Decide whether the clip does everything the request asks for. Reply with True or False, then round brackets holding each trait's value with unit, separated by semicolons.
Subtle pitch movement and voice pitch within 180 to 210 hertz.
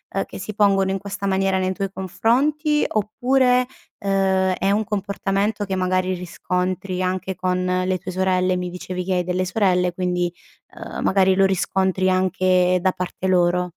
True (1.2 semitones; 190 Hz)